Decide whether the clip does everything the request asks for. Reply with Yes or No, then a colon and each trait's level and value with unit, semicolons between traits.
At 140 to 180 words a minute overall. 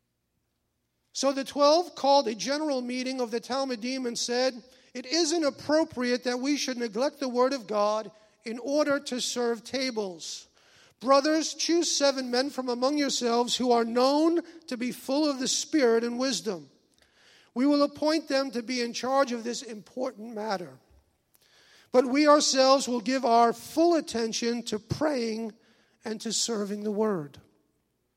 Yes: average, 155 wpm